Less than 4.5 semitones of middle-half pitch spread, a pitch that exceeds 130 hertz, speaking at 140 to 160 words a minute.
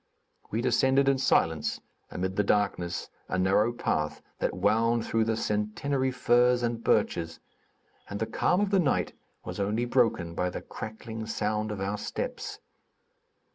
No: average, 3.7 semitones; low, 110 Hz; average, 150 wpm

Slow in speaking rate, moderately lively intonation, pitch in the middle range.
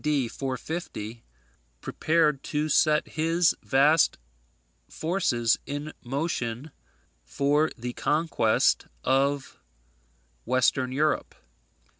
Yes: slow, 80 wpm; average, 3.3 semitones; medium, 145 Hz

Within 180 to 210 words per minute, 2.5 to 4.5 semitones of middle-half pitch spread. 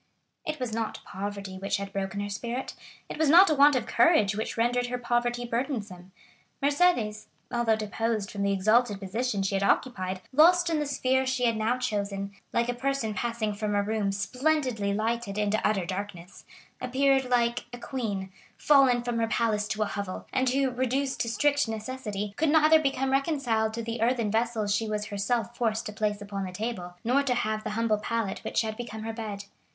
Yes: average, 190 wpm; average, 3.6 semitones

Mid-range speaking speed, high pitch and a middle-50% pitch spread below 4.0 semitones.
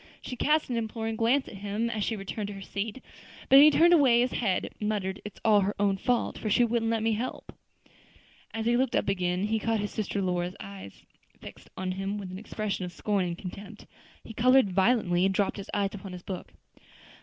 No: fast, 220 wpm; high, 210 Hz; average, 3.2 semitones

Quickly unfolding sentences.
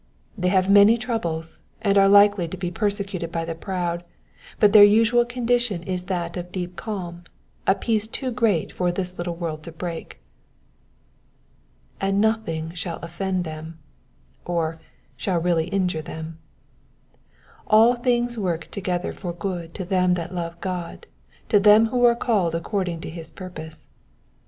No: average, 160 wpm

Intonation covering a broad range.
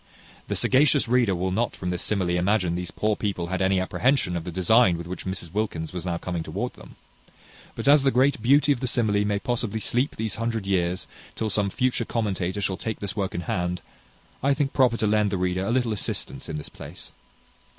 No: average, 4.7 semitones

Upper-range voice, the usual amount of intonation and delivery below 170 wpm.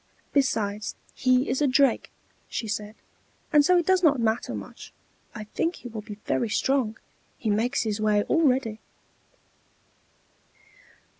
Yes: high, 240 Hz; average, 4.5 semitones; average, 140 wpm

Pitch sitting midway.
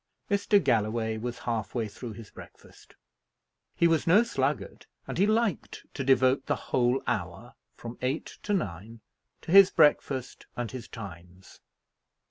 No: low, 125 Hz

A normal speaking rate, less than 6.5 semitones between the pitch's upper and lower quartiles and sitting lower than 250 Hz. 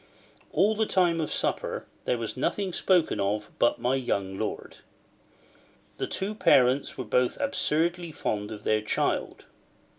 No: average, 145 wpm; wide, 8.5 semitones; low, 135 Hz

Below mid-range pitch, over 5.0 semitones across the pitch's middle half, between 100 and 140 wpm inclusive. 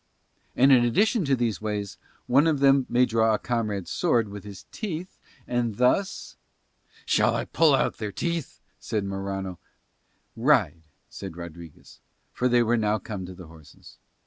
No: low, 115 Hz; wide, 5.4 semitones; average, 165 wpm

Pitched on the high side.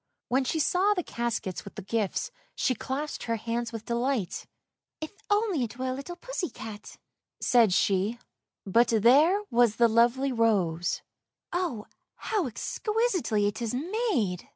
Yes: high, 240 Hz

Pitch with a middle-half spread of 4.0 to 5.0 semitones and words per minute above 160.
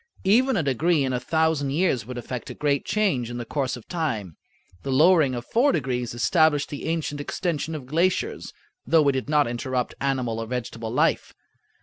Yes: average, 4.5 semitones; average, 190 wpm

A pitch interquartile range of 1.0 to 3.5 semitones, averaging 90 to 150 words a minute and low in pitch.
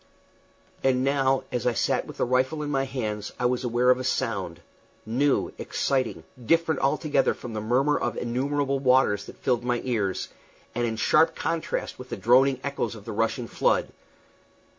No: average, 2.8 semitones; average, 175 wpm; low, 125 Hz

